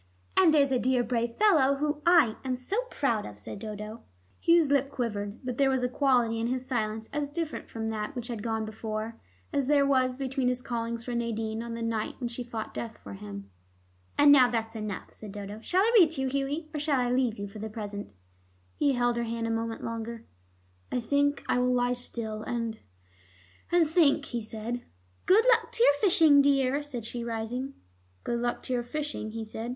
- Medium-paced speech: No, fast, 210 wpm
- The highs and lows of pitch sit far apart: No, average, 3.8 semitones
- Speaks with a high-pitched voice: Yes, high, 245 Hz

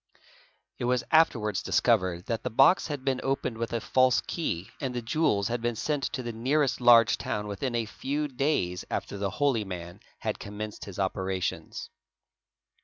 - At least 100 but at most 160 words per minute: No, average, 175 wpm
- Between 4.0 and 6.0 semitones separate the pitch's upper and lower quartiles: Yes, average, 4.8 semitones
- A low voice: Yes, low, 115 Hz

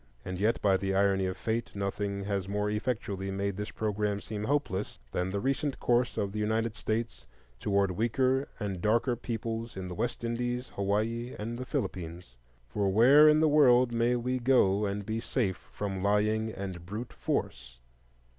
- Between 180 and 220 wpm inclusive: No, average, 170 wpm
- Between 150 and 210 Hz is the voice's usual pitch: No, low, 105 Hz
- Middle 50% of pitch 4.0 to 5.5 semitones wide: No, average, 3.3 semitones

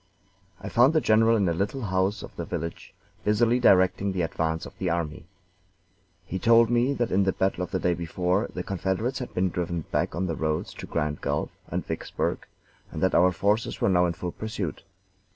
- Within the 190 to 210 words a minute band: Yes, fast, 205 wpm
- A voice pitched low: Yes, very low, 95 Hz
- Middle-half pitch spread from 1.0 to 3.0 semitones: No, average, 4.1 semitones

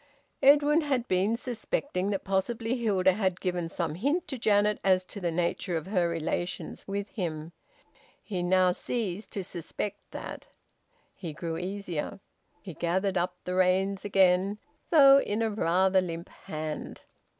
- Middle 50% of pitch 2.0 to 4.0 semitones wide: Yes, average, 3.0 semitones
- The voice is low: No, high, 190 Hz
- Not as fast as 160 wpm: Yes, average, 150 wpm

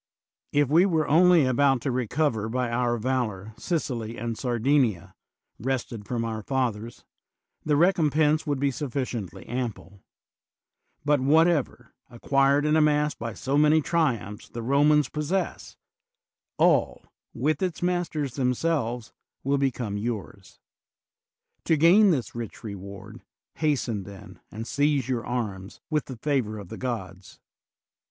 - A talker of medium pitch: No, low, 130 Hz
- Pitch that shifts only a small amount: No, average, 4.7 semitones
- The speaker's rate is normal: No, slow, 130 wpm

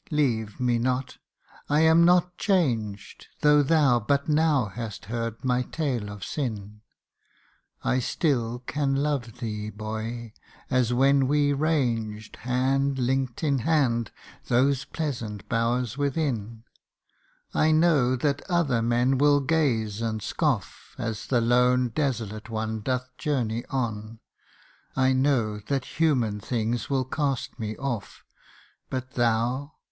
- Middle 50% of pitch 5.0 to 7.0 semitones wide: No, average, 3.8 semitones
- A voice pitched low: Yes, low, 125 Hz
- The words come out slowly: Yes, slow, 125 wpm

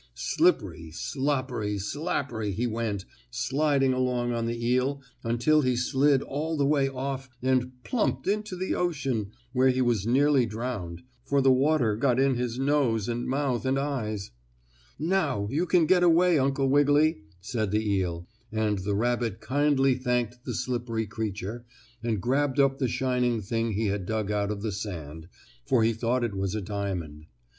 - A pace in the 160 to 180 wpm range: Yes, average, 165 wpm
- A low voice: Yes, low, 125 Hz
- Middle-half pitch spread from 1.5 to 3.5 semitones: No, average, 4.2 semitones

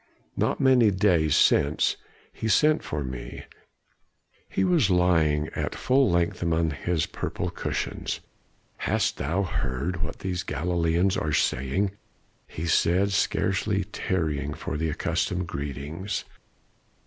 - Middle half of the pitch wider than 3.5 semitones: Yes, average, 4.2 semitones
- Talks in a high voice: No, very low, 85 Hz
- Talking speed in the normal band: No, slow, 120 wpm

